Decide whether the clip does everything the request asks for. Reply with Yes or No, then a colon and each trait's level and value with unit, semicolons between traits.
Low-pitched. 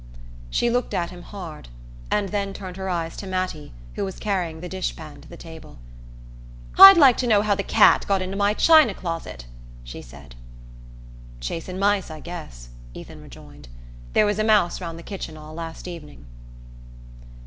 No: medium, 185 Hz